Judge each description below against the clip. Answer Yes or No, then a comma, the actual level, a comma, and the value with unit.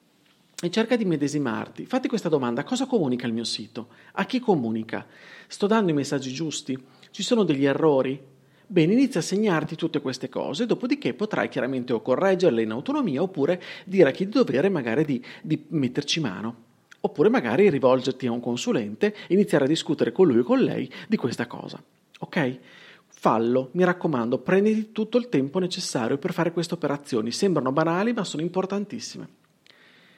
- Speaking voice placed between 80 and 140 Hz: No, medium, 170 Hz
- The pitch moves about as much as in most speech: No, wide, 7.4 semitones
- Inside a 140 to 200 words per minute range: Yes, fast, 170 wpm